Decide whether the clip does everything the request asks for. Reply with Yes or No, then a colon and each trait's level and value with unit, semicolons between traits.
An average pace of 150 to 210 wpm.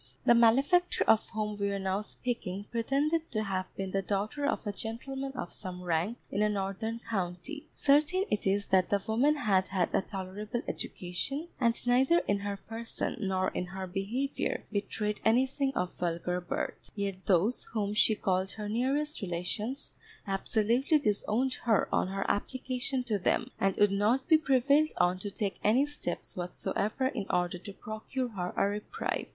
Yes: average, 170 wpm